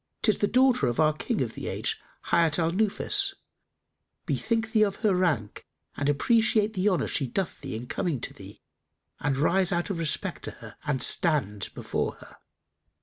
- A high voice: No, medium, 175 Hz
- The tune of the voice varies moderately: No, wide, 6.6 semitones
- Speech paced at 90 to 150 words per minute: No, average, 180 wpm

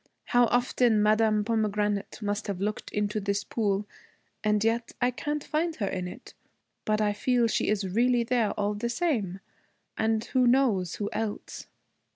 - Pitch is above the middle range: Yes, high, 215 Hz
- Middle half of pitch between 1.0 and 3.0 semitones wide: Yes, average, 2.7 semitones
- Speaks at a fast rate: No, average, 165 wpm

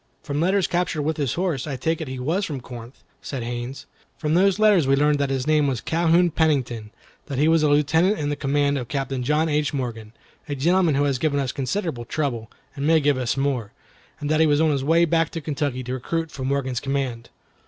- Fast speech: Yes, fast, 225 wpm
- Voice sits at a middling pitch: Yes, medium, 145 Hz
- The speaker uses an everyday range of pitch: Yes, average, 3.5 semitones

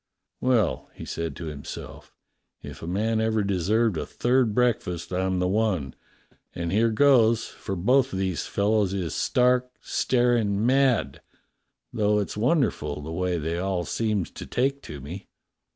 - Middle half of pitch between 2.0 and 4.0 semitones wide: No, average, 4.9 semitones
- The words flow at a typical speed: Yes, average, 155 wpm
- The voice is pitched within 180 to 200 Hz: No, low, 105 Hz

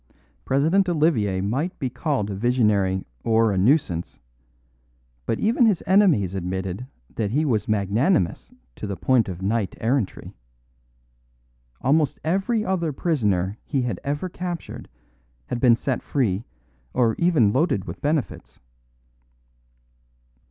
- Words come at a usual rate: No, slow, 125 wpm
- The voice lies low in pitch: Yes, low, 125 Hz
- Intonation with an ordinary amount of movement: No, wide, 7.8 semitones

